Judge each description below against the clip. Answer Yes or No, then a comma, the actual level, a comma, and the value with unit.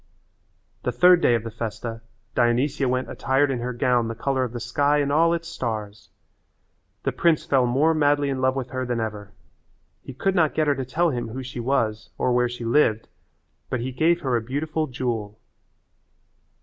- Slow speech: No, average, 195 wpm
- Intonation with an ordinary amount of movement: Yes, average, 3.6 semitones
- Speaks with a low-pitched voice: Yes, low, 130 Hz